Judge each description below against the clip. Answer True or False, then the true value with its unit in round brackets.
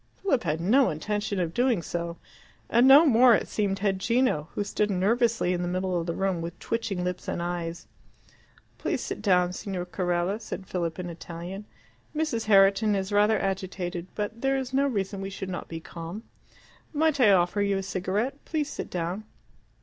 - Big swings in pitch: False (4.1 semitones)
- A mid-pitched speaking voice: False (195 Hz)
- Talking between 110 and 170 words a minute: False (185 wpm)